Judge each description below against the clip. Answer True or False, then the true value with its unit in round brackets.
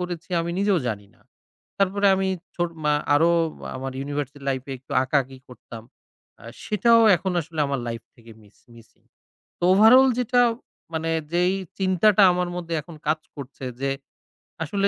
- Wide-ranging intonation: True (6.0 semitones)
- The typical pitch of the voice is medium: True (165 Hz)